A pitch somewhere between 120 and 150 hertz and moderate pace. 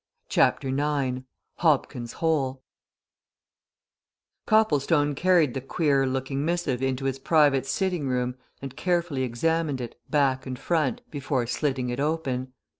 No: low, 135 Hz; slow, 120 wpm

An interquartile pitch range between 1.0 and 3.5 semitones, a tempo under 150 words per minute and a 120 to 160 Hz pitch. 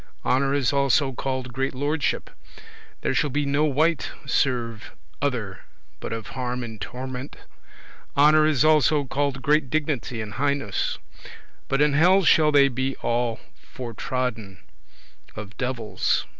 Yes: average, 2.9 semitones; average, 140 wpm; low, 135 Hz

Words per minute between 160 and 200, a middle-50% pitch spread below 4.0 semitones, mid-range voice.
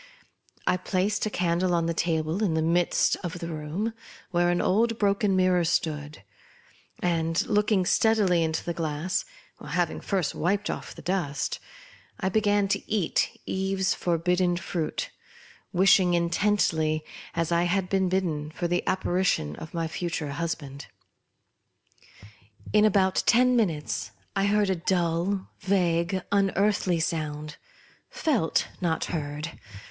No: slow, 135 wpm; average, 3.0 semitones; medium, 175 Hz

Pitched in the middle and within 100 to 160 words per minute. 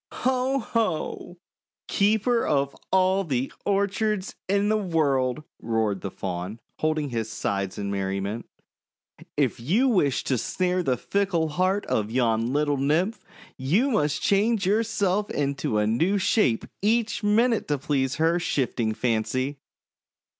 Yes: medium, 155 Hz; average, 140 wpm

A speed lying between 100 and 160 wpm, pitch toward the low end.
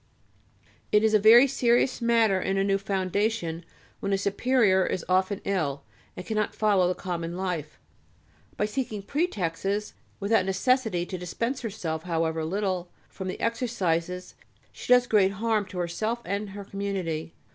No: average, 150 wpm; high, 195 Hz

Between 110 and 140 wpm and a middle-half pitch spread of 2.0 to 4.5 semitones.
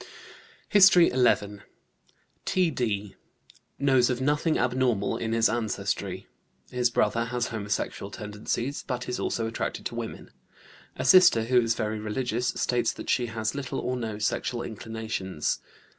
Yes: slow, 135 wpm; narrow, 2.6 semitones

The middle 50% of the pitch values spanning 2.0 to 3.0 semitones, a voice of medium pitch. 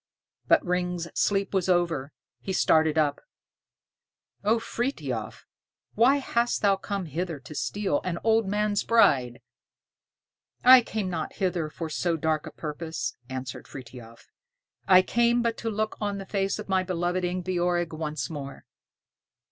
No: average, 4.5 semitones; medium, 180 Hz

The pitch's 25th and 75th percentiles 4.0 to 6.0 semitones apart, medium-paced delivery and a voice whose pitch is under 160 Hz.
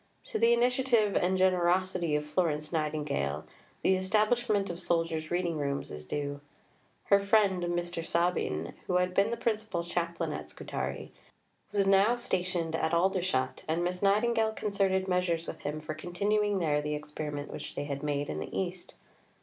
No: average, 4.5 semitones; average, 160 wpm; medium, 175 Hz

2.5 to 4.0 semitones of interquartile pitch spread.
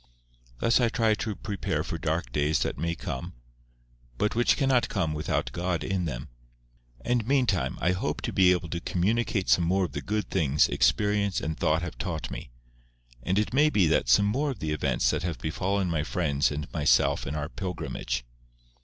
No: average, 5.1 semitones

